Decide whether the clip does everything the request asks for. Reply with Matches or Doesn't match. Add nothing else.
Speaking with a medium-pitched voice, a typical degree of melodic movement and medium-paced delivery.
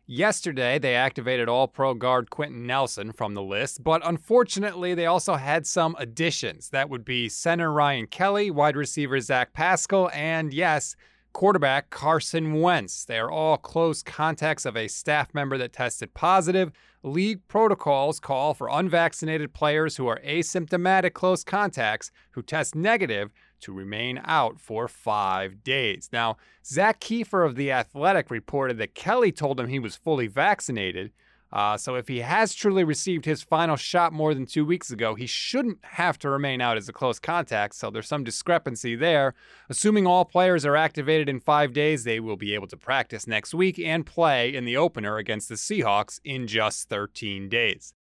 Doesn't match